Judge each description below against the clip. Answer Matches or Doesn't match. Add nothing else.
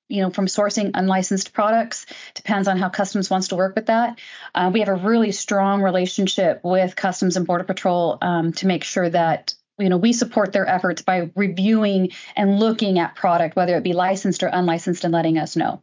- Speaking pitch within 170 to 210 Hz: Matches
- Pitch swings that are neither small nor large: Doesn't match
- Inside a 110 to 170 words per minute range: Doesn't match